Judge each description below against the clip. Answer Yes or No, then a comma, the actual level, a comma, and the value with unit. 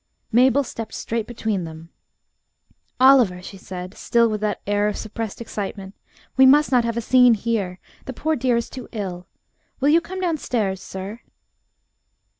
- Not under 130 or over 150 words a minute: No, average, 160 wpm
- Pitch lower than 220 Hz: No, high, 225 Hz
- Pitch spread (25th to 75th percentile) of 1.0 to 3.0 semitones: No, average, 4.7 semitones